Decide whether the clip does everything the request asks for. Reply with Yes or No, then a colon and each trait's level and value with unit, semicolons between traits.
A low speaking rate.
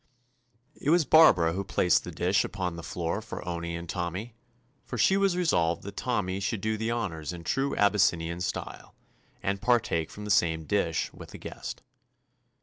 No: average, 180 wpm